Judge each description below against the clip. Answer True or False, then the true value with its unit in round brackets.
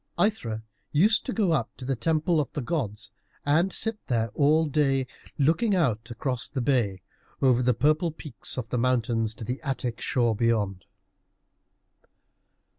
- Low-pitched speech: True (130 Hz)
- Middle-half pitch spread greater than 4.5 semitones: True (5.1 semitones)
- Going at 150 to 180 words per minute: True (155 wpm)